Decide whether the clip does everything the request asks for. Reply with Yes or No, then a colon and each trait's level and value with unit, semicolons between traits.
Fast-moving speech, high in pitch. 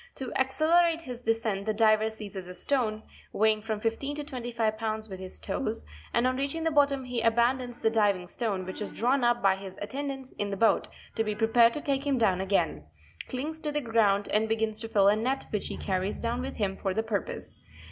Yes: fast, 220 wpm; high, 225 Hz